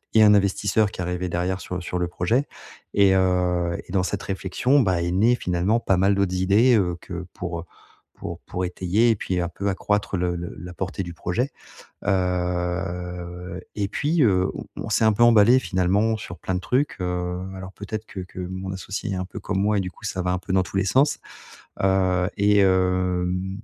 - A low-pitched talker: Yes, very low, 95 Hz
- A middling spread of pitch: No, narrow, 2.3 semitones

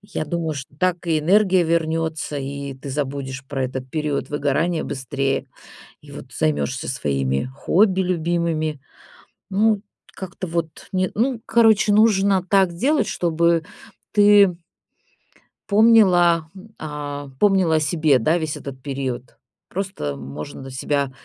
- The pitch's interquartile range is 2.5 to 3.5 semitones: No, average, 5.1 semitones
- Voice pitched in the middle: Yes, medium, 160 Hz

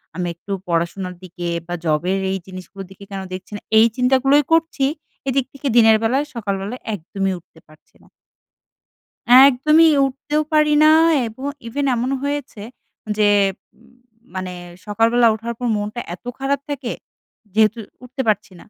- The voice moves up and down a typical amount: No, wide, 5.8 semitones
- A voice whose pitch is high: Yes, high, 230 Hz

